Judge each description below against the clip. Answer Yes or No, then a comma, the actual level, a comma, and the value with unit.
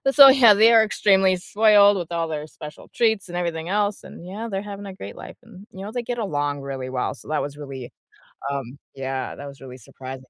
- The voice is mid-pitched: Yes, medium, 175 Hz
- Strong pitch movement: Yes, wide, 6.7 semitones